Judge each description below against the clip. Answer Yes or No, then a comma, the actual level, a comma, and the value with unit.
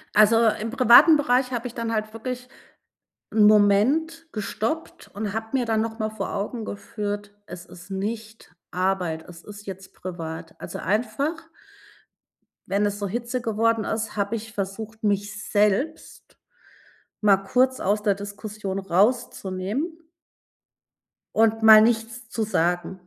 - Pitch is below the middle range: No, high, 215 Hz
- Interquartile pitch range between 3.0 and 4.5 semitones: No, narrow, 2.5 semitones